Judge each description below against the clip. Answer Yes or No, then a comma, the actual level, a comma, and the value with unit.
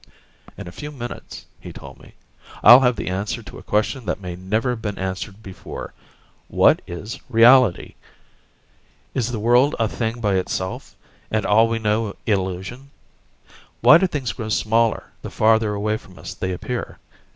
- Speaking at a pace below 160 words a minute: No, average, 165 wpm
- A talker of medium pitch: No, low, 110 Hz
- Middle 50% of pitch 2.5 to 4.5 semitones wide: Yes, average, 3.7 semitones